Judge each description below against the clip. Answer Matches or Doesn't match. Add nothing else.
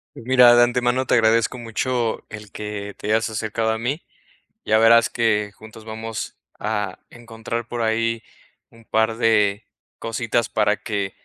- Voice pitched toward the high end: Doesn't match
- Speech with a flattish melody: Matches